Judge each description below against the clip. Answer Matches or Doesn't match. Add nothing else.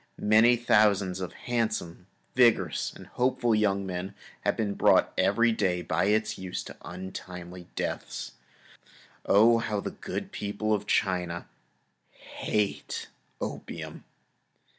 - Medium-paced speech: Doesn't match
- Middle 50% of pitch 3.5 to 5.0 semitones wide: Doesn't match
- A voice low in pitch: Matches